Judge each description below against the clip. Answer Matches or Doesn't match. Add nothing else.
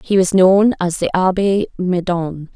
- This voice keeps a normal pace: Matches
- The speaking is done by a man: Doesn't match